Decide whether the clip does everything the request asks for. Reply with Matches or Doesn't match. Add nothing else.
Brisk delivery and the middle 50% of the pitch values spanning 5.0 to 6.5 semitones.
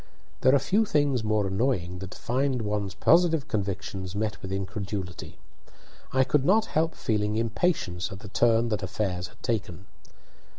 Doesn't match